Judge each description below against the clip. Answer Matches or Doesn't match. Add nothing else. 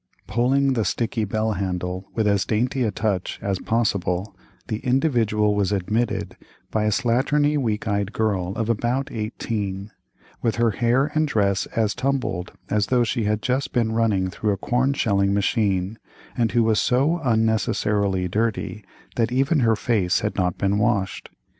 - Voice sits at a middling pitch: Doesn't match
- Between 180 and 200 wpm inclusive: Doesn't match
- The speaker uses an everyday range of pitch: Matches